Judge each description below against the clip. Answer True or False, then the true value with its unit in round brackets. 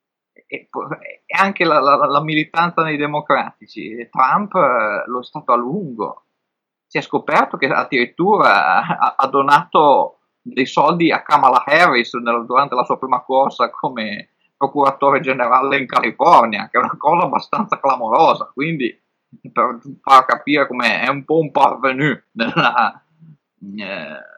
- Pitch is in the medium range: True (145 Hz)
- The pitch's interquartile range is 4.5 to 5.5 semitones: False (3.1 semitones)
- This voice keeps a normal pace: True (140 wpm)